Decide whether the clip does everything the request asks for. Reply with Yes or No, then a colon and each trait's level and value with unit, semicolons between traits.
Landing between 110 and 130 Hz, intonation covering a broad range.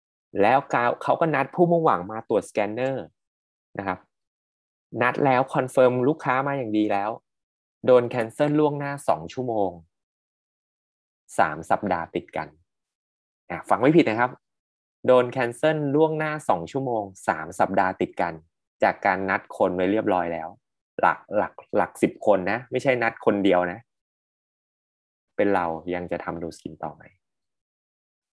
Yes: low, 120 Hz; wide, 7.5 semitones